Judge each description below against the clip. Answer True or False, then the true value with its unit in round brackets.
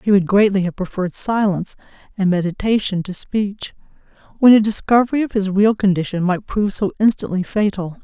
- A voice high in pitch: True (200 Hz)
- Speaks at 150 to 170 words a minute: True (165 wpm)